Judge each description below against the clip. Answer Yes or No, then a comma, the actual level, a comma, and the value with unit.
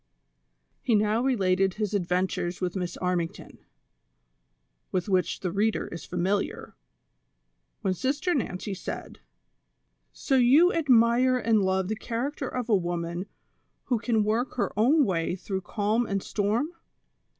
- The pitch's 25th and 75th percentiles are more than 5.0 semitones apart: No, average, 4.7 semitones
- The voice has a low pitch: No, high, 205 Hz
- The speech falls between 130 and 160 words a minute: Yes, slow, 135 wpm